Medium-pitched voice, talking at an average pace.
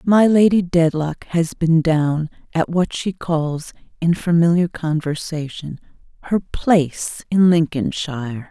No: medium, 165 Hz; slow, 120 wpm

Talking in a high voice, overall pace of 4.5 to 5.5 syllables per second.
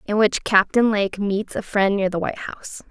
Yes: high, 200 Hz; 5.1 syllables/s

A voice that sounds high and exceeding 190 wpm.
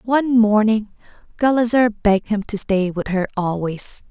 No: high, 215 Hz; average, 145 wpm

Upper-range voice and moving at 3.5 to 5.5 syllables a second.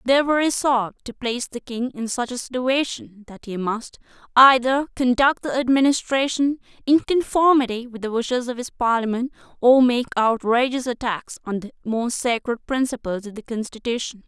Yes: high, 245 Hz; 5.2 syllables/s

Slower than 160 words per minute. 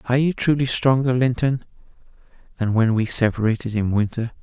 Yes: average, 150 wpm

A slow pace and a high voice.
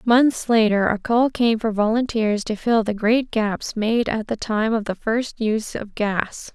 No: average, 200 wpm; high, 220 Hz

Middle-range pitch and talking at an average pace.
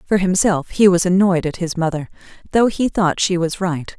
No: medium, 180 Hz; fast, 210 wpm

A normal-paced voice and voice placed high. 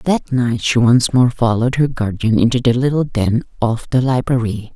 No: average, 190 wpm; low, 120 Hz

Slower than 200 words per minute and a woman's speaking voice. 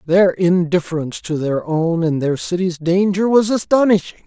No: average, 155 wpm; male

